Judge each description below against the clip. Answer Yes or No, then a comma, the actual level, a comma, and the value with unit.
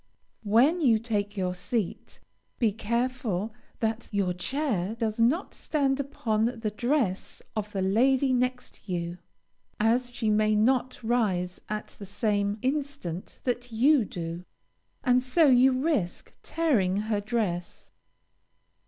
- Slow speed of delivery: Yes, slow, 125 wpm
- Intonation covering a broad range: No, average, 4.0 semitones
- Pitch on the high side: Yes, high, 225 Hz